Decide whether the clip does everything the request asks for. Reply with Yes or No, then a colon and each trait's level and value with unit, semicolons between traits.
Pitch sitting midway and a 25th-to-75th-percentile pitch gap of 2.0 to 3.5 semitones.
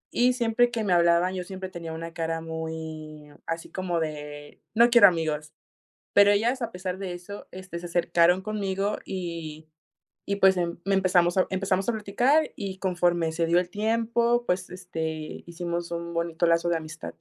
Yes: medium, 175 Hz; average, 3.1 semitones